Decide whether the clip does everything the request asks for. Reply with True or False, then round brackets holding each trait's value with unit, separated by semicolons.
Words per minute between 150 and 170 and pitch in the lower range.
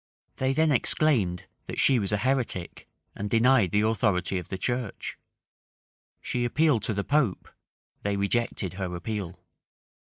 False (140 wpm; 110 Hz)